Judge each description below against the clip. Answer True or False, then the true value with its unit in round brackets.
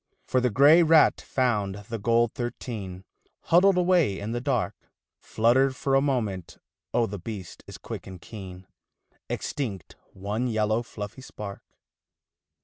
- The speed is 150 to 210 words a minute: False (140 wpm)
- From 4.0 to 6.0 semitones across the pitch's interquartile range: True (4.6 semitones)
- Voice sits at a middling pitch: False (115 Hz)